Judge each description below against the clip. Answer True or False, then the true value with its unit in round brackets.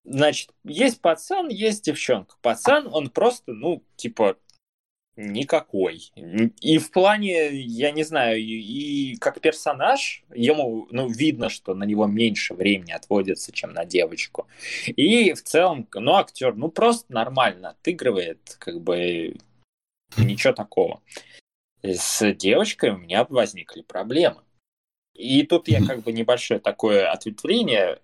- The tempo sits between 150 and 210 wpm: False (130 wpm)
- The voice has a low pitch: False (155 Hz)